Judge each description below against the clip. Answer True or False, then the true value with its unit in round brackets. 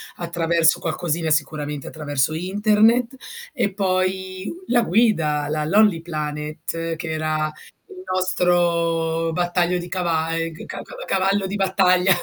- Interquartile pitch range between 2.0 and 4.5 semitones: True (2.9 semitones)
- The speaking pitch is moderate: True (170 Hz)